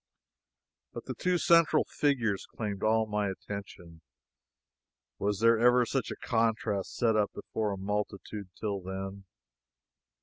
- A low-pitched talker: Yes, low, 105 Hz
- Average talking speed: No, slow, 125 wpm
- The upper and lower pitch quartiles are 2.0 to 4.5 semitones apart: Yes, average, 2.7 semitones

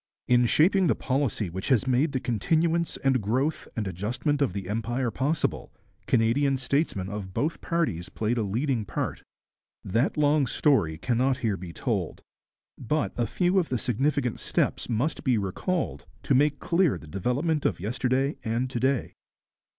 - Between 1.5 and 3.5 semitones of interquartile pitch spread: No, average, 4.8 semitones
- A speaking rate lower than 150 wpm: No, average, 160 wpm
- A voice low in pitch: Yes, low, 125 Hz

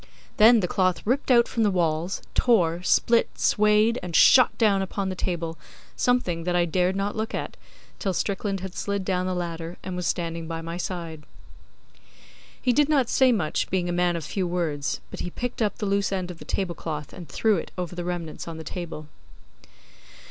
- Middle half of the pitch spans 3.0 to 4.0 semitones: Yes, average, 3.6 semitones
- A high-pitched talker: No, medium, 180 Hz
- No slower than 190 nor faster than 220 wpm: Yes, average, 200 wpm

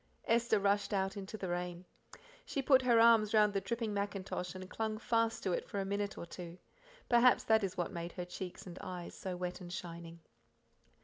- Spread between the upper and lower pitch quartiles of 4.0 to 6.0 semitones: No, average, 3.6 semitones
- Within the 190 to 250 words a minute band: Yes, average, 200 wpm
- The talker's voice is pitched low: No, high, 195 Hz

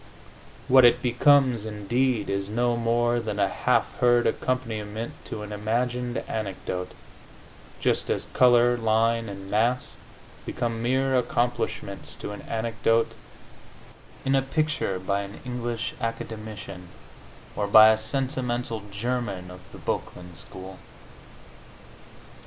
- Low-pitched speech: Yes, low, 115 Hz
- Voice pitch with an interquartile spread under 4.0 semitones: Yes, average, 2.9 semitones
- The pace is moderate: No, slow, 120 wpm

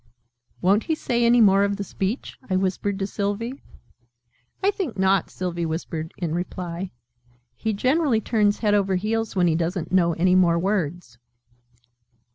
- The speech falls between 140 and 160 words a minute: Yes, average, 155 wpm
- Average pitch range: Yes, average, 3.4 semitones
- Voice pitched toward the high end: Yes, high, 195 Hz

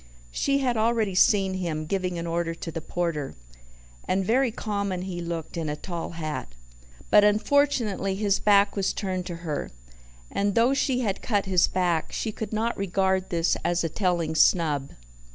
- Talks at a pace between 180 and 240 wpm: No, average, 170 wpm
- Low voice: No, high, 190 Hz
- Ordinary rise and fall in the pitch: Yes, average, 3.7 semitones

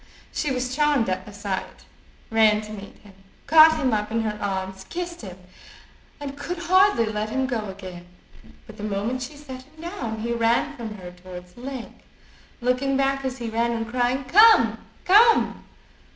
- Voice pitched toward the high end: Yes, high, 235 Hz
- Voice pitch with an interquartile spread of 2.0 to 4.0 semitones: No, average, 4.9 semitones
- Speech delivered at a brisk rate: No, average, 180 wpm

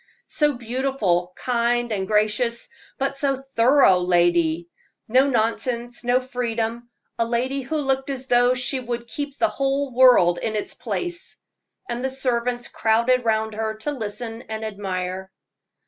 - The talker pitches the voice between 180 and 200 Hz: No, high, 240 Hz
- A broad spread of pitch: No, average, 3.3 semitones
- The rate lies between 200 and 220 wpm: No, average, 145 wpm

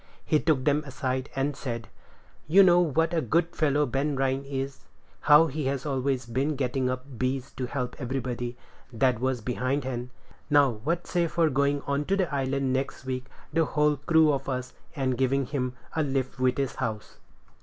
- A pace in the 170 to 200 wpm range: Yes, average, 180 wpm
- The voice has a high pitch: No, low, 135 Hz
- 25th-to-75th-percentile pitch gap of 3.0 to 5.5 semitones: No, narrow, 2.5 semitones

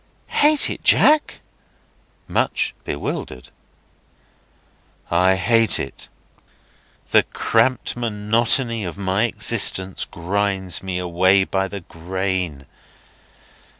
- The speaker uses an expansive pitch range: No, average, 3.9 semitones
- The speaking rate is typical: No, slow, 85 wpm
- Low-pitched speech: Yes, very low, 95 Hz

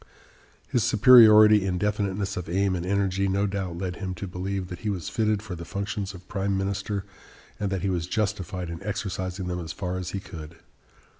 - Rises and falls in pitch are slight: Yes, narrow, 2.0 semitones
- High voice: No, very low, 95 Hz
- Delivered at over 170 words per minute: Yes, average, 200 wpm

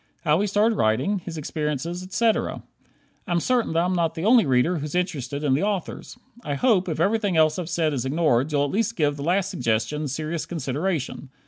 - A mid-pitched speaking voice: Yes, medium, 165 Hz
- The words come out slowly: No, average, 200 wpm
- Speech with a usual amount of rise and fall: Yes, average, 4.5 semitones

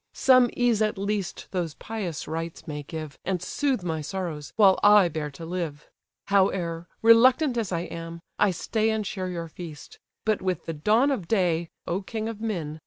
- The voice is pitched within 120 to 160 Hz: No, medium, 185 Hz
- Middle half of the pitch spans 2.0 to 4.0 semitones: No, average, 4.7 semitones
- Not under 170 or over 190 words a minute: Yes, average, 180 wpm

